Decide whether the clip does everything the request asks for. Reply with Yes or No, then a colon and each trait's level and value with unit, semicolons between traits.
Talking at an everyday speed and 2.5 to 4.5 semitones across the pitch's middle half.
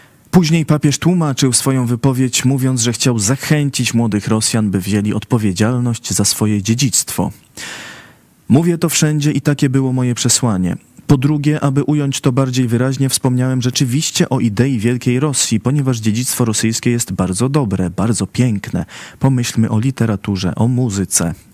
Yes: average, 140 wpm; average, 3.9 semitones